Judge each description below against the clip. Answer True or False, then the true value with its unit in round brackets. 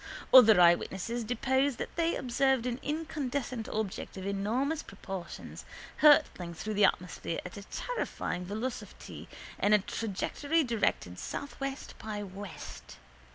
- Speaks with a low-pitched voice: False (225 Hz)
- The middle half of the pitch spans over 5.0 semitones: True (5.6 semitones)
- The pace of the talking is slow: True (120 wpm)